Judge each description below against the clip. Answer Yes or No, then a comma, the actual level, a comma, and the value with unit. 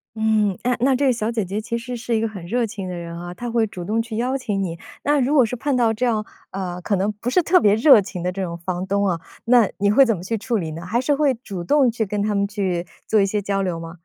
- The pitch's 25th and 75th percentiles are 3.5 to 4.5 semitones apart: Yes, average, 4.2 semitones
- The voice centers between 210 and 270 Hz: Yes, high, 215 Hz